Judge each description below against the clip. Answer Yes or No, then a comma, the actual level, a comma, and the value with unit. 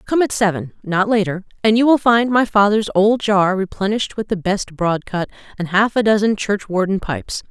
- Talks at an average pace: Yes, average, 190 wpm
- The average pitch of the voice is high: Yes, high, 205 Hz